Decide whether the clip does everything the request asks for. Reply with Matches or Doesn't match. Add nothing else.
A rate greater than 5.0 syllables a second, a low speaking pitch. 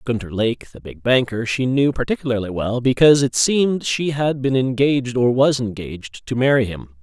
Matches